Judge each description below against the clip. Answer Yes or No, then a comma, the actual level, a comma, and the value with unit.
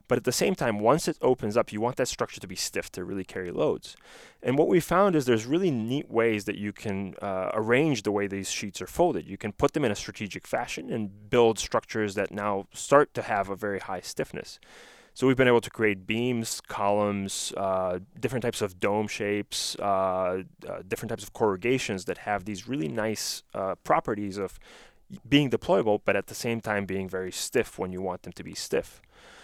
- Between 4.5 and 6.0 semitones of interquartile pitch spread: No, average, 2.8 semitones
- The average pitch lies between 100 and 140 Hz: Yes, low, 105 Hz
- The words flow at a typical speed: No, fast, 215 wpm